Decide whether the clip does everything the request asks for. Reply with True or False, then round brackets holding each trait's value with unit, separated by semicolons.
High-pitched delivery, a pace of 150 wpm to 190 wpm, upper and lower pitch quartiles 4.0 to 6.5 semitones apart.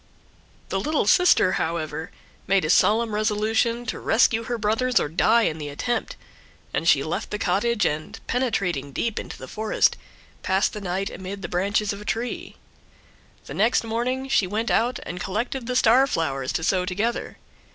True (210 Hz; 170 wpm; 4.4 semitones)